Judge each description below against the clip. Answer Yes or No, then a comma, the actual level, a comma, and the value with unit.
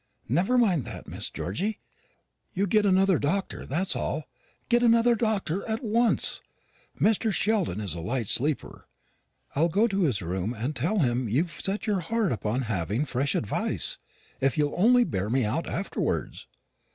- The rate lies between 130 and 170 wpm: Yes, average, 160 wpm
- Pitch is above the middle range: No, medium, 170 Hz